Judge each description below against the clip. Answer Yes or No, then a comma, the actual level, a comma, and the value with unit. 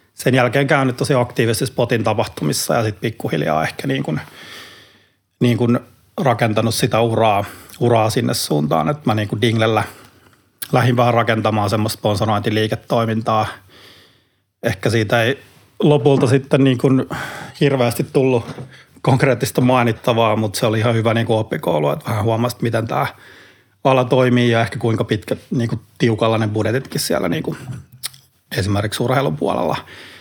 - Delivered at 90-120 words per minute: No, average, 135 wpm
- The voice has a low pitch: Yes, low, 120 Hz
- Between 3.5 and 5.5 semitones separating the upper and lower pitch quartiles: No, average, 2.7 semitones